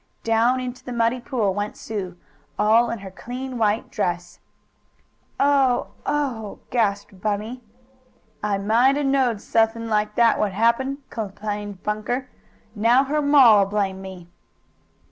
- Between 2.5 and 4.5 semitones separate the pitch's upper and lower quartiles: Yes, average, 3.5 semitones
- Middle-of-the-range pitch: No, high, 225 Hz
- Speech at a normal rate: No, slow, 125 wpm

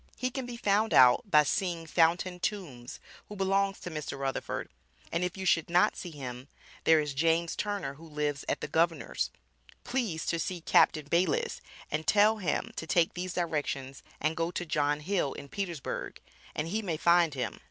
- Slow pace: No, average, 185 wpm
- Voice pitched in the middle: Yes, medium, 165 Hz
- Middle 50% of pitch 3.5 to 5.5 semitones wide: Yes, average, 4.0 semitones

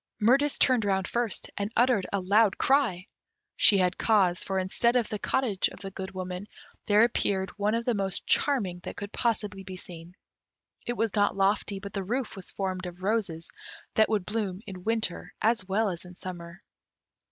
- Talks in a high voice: Yes, high, 200 Hz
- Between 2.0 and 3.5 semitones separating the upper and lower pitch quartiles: Yes, average, 3.2 semitones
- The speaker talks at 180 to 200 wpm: Yes, average, 185 wpm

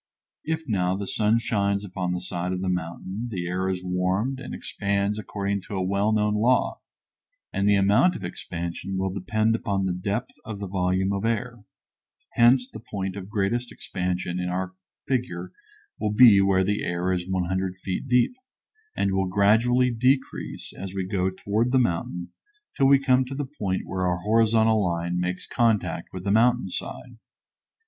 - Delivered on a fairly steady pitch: No, average, 3.6 semitones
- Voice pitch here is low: Yes, low, 100 Hz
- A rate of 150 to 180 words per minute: Yes, average, 175 wpm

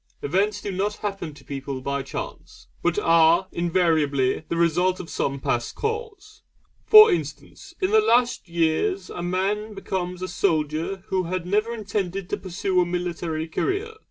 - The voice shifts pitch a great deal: No, average, 4.1 semitones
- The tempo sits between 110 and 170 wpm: Yes, average, 155 wpm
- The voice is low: No, medium, 185 Hz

